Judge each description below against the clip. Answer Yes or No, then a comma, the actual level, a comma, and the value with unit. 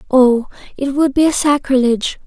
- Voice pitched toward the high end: Yes, very high, 270 Hz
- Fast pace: No, average, 160 wpm